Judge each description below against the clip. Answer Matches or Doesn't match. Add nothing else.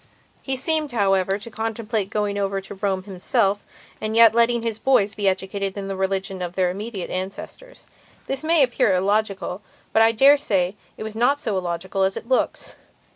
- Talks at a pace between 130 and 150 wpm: Doesn't match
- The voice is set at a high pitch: Matches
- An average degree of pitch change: Matches